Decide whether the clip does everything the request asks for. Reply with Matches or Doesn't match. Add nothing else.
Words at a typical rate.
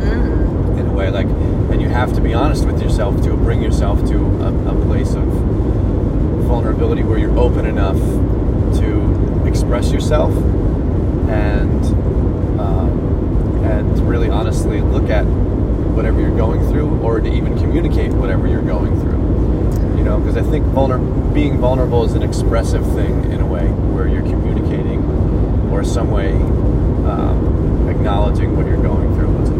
Matches